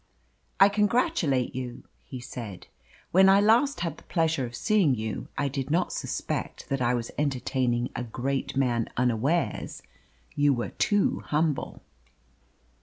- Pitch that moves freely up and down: Yes, wide, 5.9 semitones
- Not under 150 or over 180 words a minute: No, average, 140 wpm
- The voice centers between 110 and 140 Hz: Yes, low, 135 Hz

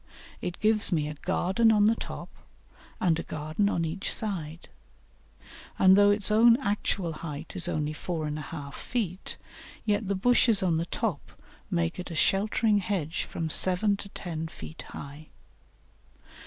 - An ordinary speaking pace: Yes, average, 155 wpm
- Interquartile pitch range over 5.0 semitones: No, average, 4.6 semitones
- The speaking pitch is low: No, medium, 185 Hz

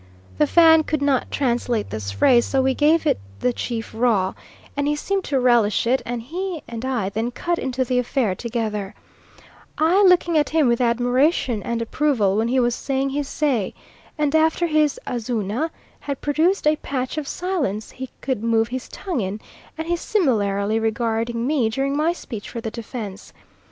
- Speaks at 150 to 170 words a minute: No, average, 180 wpm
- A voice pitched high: Yes, very high, 250 Hz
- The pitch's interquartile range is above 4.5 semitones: Yes, average, 5.0 semitones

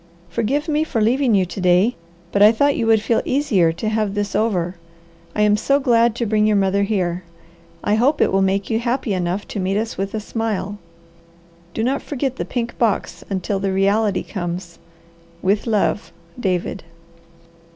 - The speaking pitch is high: Yes, high, 210 Hz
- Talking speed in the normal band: Yes, average, 185 wpm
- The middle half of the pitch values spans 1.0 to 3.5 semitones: Yes, average, 3.2 semitones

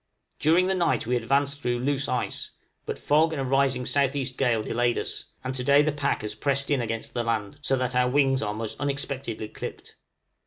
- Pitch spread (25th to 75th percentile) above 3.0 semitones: No, average, 2.7 semitones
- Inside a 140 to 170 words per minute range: No, fast, 205 wpm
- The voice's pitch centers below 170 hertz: Yes, low, 135 Hz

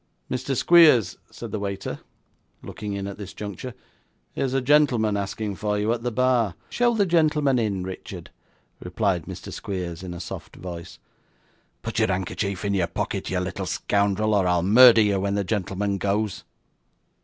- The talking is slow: No, average, 165 wpm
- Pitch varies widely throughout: No, average, 4.1 semitones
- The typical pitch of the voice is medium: No, low, 100 Hz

